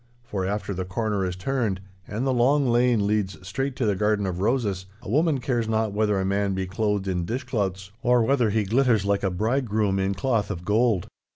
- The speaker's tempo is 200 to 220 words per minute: Yes, fast, 205 wpm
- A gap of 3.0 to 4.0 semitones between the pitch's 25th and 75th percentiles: Yes, average, 3.7 semitones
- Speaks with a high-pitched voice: No, low, 105 Hz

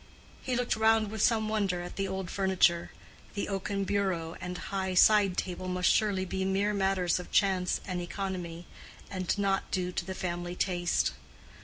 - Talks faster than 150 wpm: Yes, average, 170 wpm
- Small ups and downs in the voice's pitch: Yes, narrow, 2.0 semitones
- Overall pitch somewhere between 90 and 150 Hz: No, high, 190 Hz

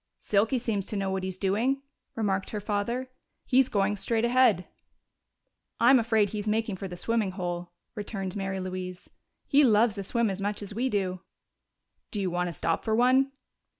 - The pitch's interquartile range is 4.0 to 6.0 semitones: No, average, 3.4 semitones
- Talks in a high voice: Yes, high, 205 Hz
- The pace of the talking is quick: No, average, 180 wpm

